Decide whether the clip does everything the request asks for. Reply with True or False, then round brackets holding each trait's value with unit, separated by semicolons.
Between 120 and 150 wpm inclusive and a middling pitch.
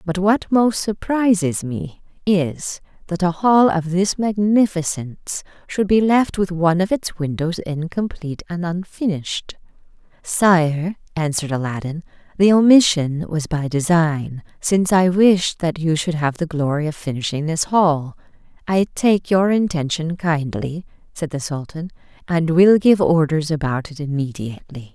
True (140 wpm; 170 Hz)